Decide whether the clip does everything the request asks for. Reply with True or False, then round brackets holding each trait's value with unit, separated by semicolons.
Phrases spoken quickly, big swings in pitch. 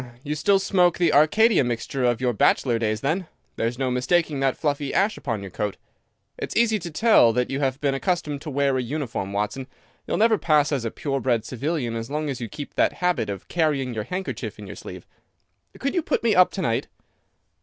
True (220 wpm; 6.1 semitones)